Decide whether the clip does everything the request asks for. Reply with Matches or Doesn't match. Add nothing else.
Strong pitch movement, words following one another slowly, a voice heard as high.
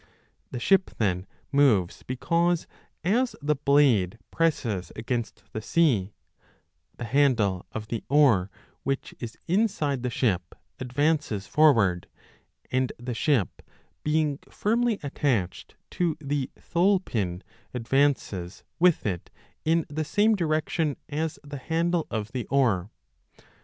Doesn't match